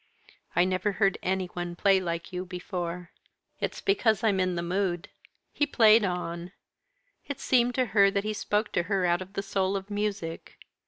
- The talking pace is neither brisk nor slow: Yes, average, 180 wpm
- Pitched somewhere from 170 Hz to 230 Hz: Yes, high, 190 Hz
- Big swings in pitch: No, average, 2.7 semitones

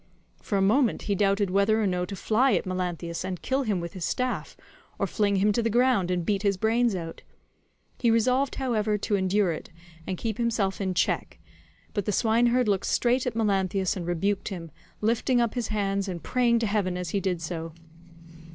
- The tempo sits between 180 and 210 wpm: Yes, average, 200 wpm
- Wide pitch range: No, average, 3.7 semitones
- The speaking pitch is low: No, high, 200 Hz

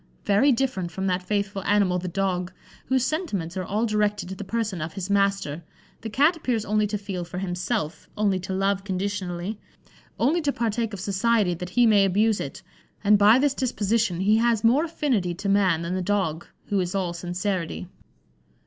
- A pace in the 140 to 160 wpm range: No, average, 185 wpm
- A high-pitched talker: Yes, high, 200 Hz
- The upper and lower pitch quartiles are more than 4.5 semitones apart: No, average, 3.4 semitones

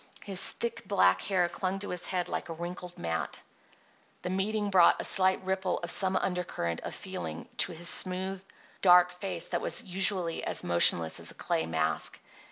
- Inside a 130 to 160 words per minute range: No, average, 175 wpm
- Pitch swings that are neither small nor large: No, narrow, 2.1 semitones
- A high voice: No, medium, 180 Hz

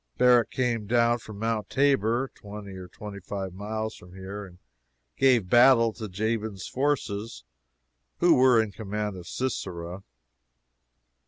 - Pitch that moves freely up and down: No, average, 3.3 semitones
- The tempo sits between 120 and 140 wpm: Yes, slow, 135 wpm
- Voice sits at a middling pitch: No, low, 110 Hz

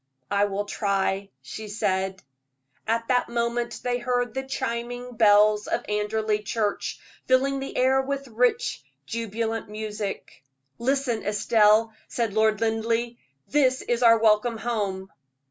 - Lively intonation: No, average, 2.7 semitones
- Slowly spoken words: Yes, slow, 130 wpm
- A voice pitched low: No, high, 225 Hz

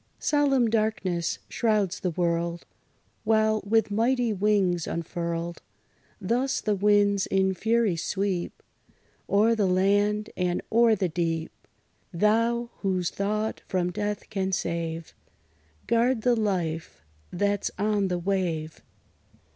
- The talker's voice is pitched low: No, high, 200 Hz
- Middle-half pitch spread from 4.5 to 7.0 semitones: No, average, 3.6 semitones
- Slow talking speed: Yes, slow, 115 wpm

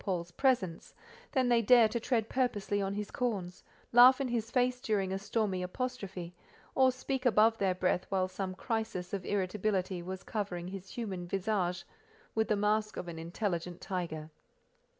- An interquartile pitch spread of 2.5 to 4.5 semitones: Yes, average, 4.0 semitones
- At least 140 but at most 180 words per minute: Yes, average, 160 wpm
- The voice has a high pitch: Yes, high, 200 Hz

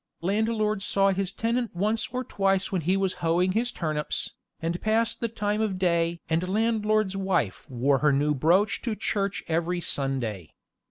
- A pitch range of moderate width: Yes, average, 4.4 semitones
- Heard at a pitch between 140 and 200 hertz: Yes, high, 190 Hz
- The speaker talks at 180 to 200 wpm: No, average, 170 wpm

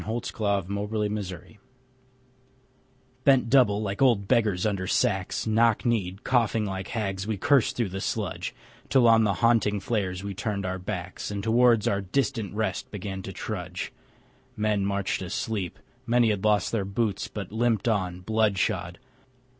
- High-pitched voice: No, low, 105 Hz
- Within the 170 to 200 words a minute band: No, average, 155 wpm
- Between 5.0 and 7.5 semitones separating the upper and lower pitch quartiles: No, average, 2.7 semitones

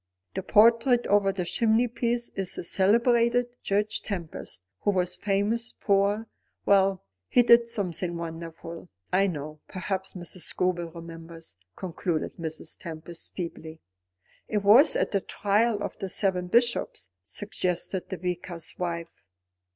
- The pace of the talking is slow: Yes, slow, 130 wpm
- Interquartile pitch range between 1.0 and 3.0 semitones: No, average, 4.1 semitones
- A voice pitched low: No, high, 190 Hz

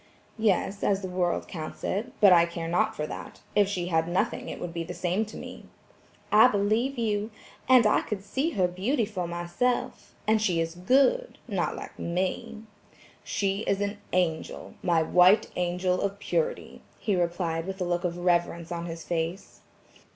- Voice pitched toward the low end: No, medium, 185 Hz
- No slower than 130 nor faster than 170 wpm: No, average, 180 wpm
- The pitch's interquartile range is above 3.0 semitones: Yes, average, 3.5 semitones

